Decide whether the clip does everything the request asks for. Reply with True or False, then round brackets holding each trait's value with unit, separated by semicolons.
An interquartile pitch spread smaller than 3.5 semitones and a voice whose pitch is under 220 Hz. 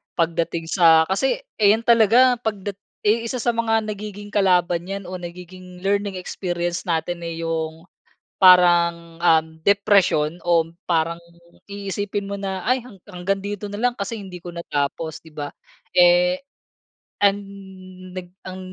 True (3.0 semitones; 185 Hz)